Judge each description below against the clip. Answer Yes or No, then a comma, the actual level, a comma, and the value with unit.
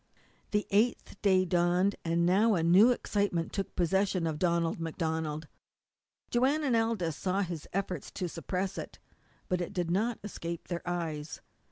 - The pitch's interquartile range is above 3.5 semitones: No, average, 3.2 semitones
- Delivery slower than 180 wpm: Yes, average, 155 wpm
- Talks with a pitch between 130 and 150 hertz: No, medium, 180 Hz